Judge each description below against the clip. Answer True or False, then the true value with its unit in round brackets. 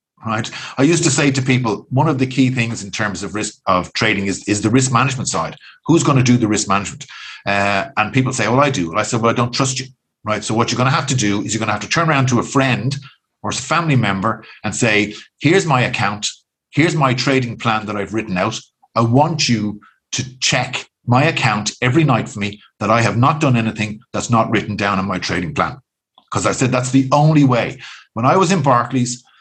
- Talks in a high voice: False (120 Hz)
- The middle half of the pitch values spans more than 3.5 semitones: True (4.0 semitones)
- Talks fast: True (245 wpm)